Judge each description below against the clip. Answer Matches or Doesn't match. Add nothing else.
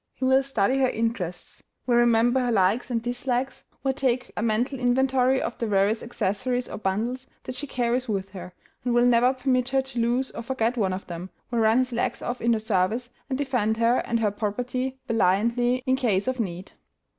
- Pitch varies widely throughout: Doesn't match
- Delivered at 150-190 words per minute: Doesn't match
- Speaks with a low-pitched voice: Doesn't match